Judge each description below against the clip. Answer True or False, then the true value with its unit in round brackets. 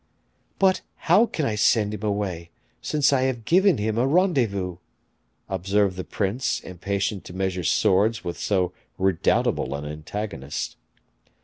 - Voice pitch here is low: True (100 Hz)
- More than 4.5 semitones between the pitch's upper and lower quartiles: True (5.0 semitones)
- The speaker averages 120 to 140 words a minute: True (135 wpm)